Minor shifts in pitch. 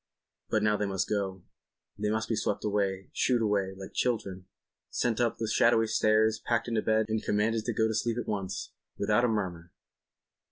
Yes: narrow, 2.2 semitones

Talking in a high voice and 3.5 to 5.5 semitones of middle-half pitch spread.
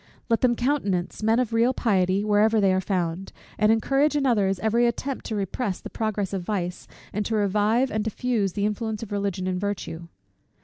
No: high, 210 Hz; average, 3.1 semitones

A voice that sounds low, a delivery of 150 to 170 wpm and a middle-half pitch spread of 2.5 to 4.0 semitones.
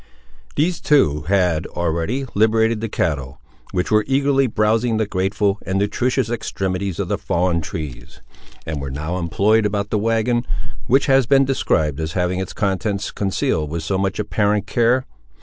No: low, 100 Hz; average, 160 wpm; average, 4.7 semitones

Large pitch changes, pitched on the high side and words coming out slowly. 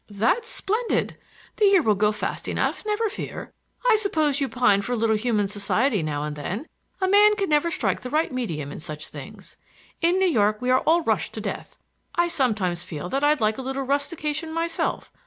No: wide, 8.3 semitones; very high, 265 Hz; fast, 205 wpm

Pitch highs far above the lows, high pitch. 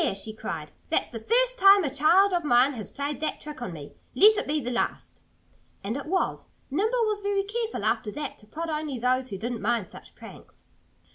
Yes: wide, 8.6 semitones; very high, 295 Hz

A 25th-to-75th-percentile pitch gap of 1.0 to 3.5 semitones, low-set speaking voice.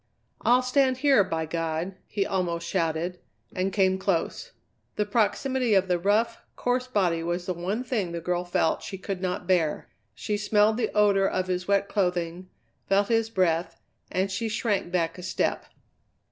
No: average, 3.2 semitones; high, 190 Hz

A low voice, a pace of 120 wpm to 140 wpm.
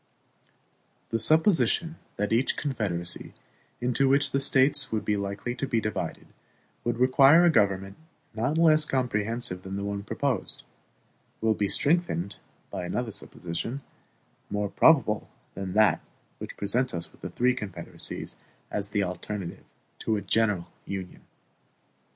Yes: low, 110 Hz; slow, 135 wpm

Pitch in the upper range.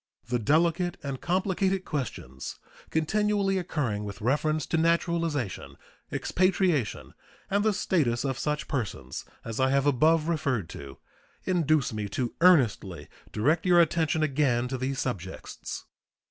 No: medium, 150 Hz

